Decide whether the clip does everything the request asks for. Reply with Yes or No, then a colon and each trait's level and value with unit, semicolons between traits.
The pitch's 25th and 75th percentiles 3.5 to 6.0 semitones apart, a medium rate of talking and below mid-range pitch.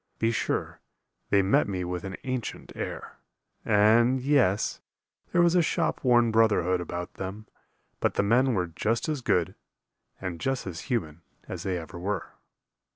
Yes: average, 5.2 semitones; average, 155 wpm; low, 105 Hz